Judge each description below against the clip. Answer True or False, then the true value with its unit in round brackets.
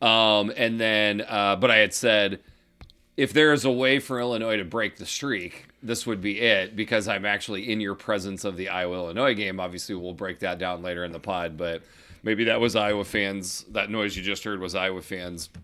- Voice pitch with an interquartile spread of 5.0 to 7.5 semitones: False (3.3 semitones)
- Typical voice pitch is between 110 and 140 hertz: False (100 Hz)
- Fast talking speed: True (220 wpm)